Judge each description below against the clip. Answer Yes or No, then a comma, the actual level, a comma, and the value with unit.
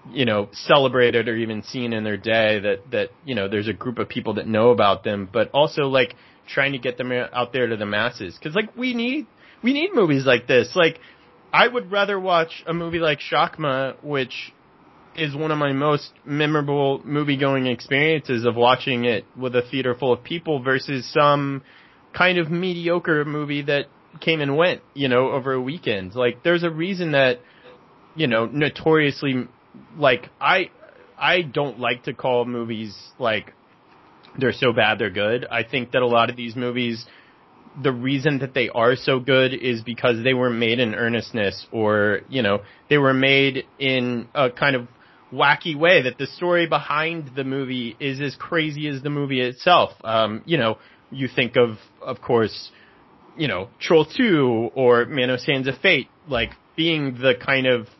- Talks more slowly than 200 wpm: Yes, average, 185 wpm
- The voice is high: No, low, 135 Hz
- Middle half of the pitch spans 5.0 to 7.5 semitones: No, average, 3.6 semitones